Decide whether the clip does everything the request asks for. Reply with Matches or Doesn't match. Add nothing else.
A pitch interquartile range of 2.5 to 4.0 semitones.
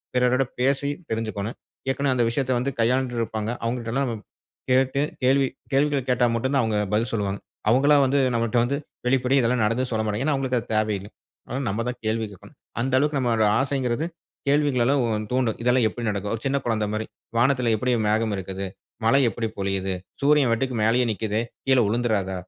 Matches